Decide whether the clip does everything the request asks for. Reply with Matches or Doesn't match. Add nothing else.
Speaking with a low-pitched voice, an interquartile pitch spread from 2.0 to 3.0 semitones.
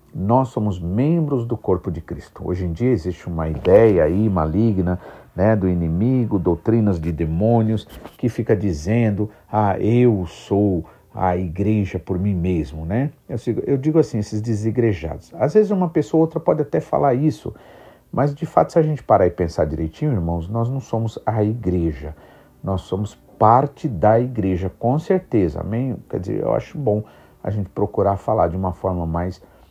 Doesn't match